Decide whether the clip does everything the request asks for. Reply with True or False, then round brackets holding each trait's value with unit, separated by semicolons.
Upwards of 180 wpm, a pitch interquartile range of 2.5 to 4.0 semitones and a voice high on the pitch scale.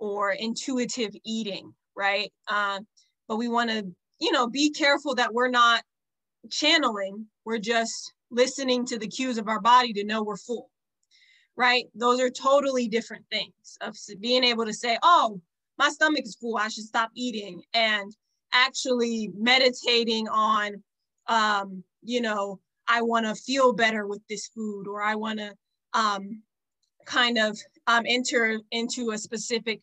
False (155 wpm; 2.8 semitones; 230 Hz)